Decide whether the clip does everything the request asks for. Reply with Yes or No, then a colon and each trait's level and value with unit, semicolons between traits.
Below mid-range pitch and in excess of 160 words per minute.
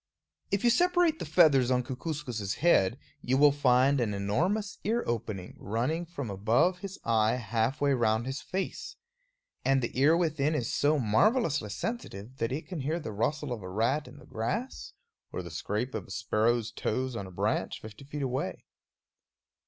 Yes: low, 130 Hz; average, 175 wpm